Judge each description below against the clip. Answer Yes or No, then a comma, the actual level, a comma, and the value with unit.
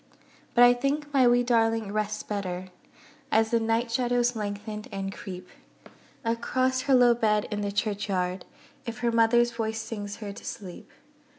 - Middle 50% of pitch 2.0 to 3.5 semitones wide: Yes, average, 2.9 semitones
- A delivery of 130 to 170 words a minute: Yes, average, 160 wpm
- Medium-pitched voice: No, high, 225 Hz